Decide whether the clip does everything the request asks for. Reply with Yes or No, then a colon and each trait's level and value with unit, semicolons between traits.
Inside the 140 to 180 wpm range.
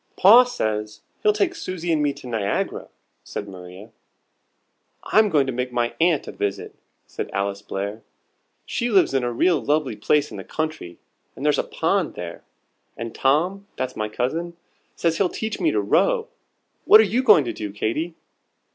Yes: average, 175 wpm